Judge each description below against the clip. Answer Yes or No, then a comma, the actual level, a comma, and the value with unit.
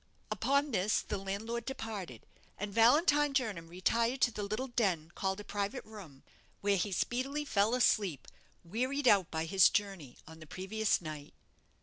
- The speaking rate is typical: Yes, average, 155 wpm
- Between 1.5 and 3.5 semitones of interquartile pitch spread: No, average, 4.7 semitones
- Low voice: No, high, 205 Hz